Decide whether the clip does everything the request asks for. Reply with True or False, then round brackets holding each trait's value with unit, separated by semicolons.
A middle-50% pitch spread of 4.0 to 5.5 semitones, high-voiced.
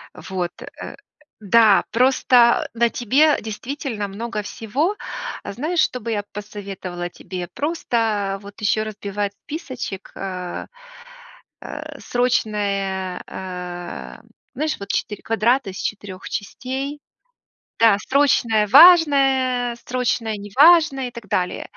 True (4.7 semitones; 220 Hz)